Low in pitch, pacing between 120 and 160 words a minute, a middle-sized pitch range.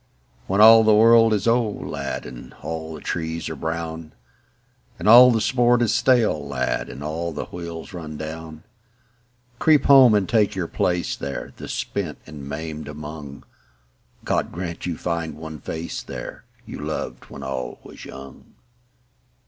No: very low, 85 Hz; average, 155 wpm; wide, 5.8 semitones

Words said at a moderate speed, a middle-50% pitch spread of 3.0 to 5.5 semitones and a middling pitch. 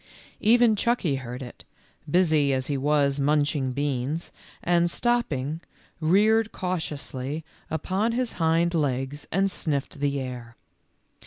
No: slow, 115 wpm; average, 4.8 semitones; medium, 150 Hz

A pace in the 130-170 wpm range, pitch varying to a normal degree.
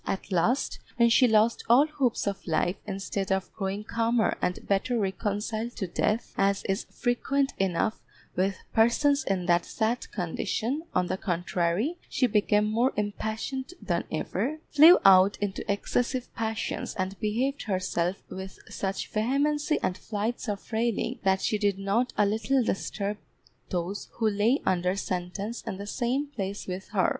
Yes: average, 155 wpm; average, 3.8 semitones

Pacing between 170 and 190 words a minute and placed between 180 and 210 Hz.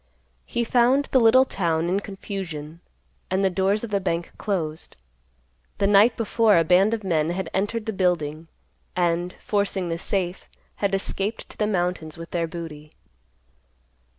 No: average, 155 wpm; high, 190 Hz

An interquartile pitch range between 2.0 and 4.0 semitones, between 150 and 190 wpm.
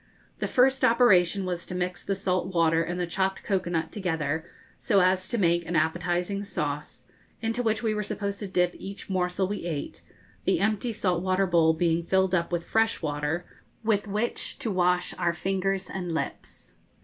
Yes: average, 2.7 semitones; average, 185 wpm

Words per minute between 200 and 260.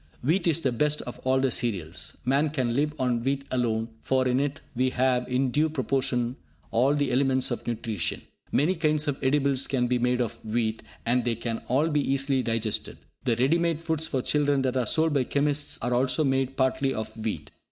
Yes: fast, 205 wpm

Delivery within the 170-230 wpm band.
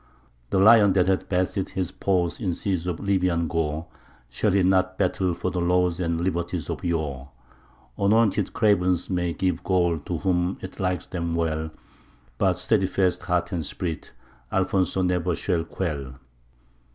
No: average, 150 wpm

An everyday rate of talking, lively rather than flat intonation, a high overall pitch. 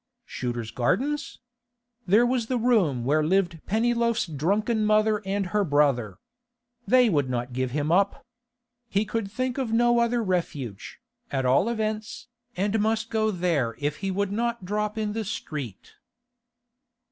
Yes: average, 145 wpm; wide, 7.2 semitones; high, 200 Hz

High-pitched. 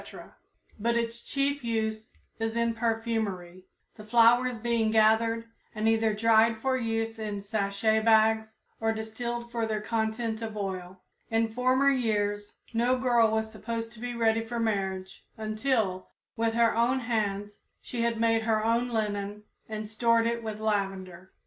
Yes: high, 225 Hz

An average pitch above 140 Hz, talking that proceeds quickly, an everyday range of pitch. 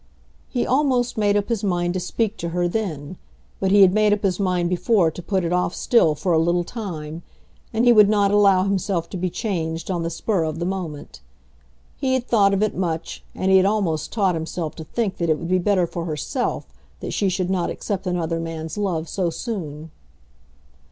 Yes: medium, 185 Hz; fast, 210 wpm; average, 3.6 semitones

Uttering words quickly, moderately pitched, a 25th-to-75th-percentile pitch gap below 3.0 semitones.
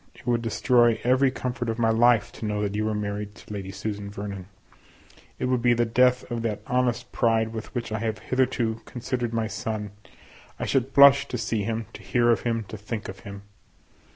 No: fast, 210 wpm; low, 115 Hz; narrow, 2.6 semitones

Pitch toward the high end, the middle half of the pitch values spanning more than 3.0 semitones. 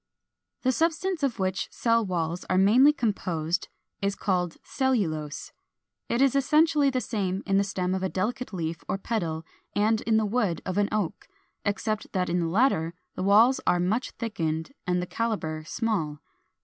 Yes: high, 200 Hz; average, 4.7 semitones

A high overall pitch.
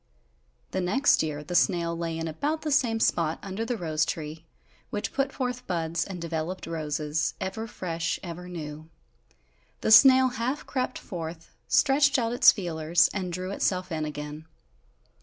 No: medium, 175 Hz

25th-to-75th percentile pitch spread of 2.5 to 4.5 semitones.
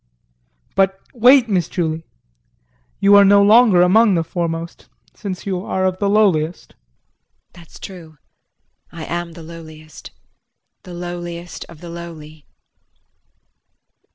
Yes: average, 3.1 semitones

